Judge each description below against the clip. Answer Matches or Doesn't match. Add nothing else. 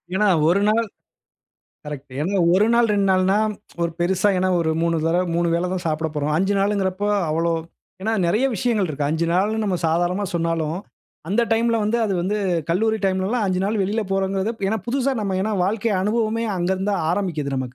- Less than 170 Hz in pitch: Doesn't match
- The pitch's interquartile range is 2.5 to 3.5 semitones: Doesn't match